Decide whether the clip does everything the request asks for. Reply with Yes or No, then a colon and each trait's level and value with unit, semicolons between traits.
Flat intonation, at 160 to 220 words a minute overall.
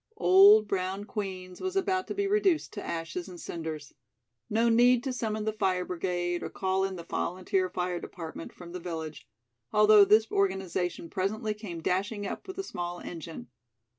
No: average, 3.6 semitones; average, 170 wpm